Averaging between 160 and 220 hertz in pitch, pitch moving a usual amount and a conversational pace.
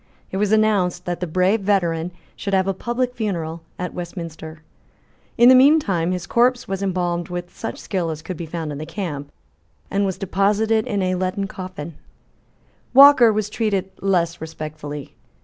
Yes: medium, 185 Hz; average, 3.7 semitones; average, 170 wpm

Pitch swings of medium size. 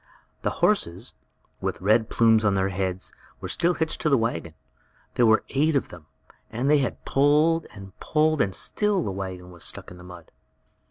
No: wide, 8.2 semitones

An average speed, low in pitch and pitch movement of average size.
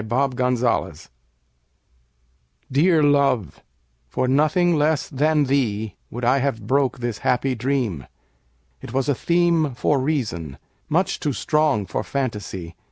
No: slow, 110 wpm; low, 130 Hz; average, 5.0 semitones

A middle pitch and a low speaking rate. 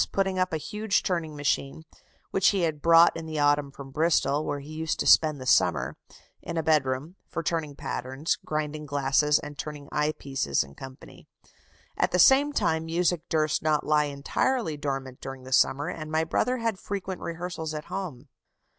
No: medium, 155 Hz; average, 180 wpm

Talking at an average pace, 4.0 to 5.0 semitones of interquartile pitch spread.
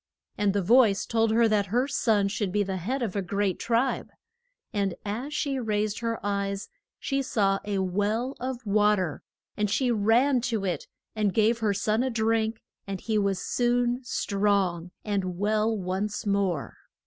No: average, 170 wpm; average, 2.7 semitones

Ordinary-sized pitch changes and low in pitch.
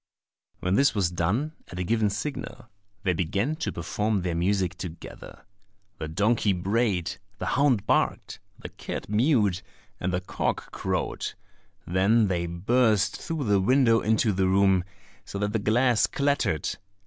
Yes: average, 4.1 semitones; low, 100 Hz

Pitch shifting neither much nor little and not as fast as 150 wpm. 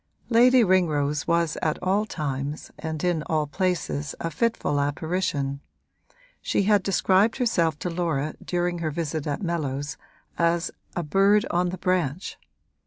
Yes: average, 3.8 semitones; average, 140 wpm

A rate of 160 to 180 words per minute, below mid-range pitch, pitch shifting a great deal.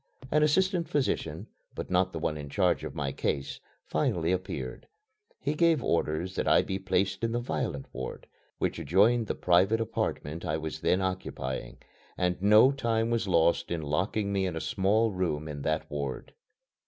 Yes: average, 175 wpm; very low, 95 Hz; wide, 6.3 semitones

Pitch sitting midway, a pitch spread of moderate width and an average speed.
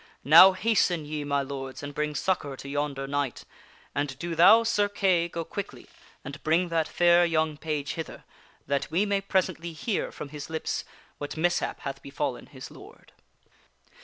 Yes: medium, 155 Hz; average, 3.7 semitones; average, 165 wpm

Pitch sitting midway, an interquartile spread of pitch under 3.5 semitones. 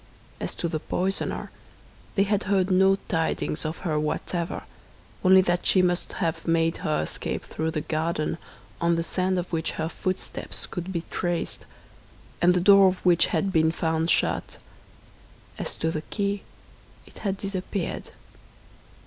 Yes: medium, 175 Hz; average, 2.7 semitones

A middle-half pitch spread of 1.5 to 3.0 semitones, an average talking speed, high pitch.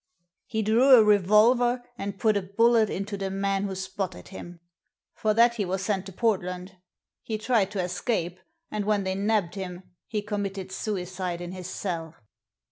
Yes: narrow, 2.6 semitones; average, 175 wpm; high, 195 Hz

